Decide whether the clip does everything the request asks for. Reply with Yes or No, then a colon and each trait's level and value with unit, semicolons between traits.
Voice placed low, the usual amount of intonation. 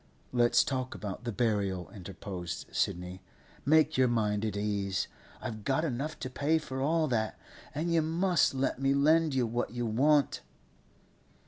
No: low, 125 Hz; wide, 6.1 semitones